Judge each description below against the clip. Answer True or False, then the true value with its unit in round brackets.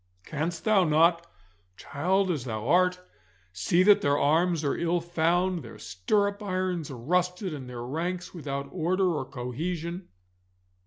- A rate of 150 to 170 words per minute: False (140 wpm)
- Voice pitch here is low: False (170 Hz)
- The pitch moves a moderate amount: True (4.3 semitones)